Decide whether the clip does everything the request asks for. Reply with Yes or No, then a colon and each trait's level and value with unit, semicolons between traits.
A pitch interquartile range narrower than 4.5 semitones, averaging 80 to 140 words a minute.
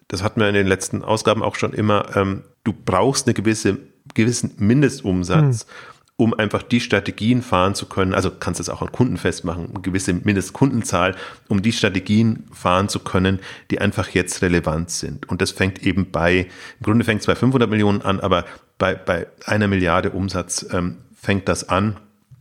No: average, 3.0 semitones; average, 180 wpm